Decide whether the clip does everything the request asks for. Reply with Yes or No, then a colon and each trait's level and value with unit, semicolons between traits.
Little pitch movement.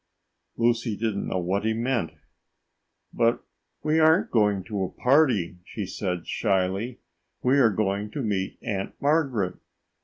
No: average, 4.4 semitones